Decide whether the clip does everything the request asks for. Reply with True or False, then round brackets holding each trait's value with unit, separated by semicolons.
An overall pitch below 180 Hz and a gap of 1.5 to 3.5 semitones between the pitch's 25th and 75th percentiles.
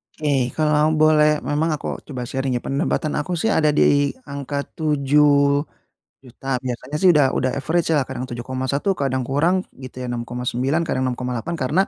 True (140 Hz; 3.0 semitones)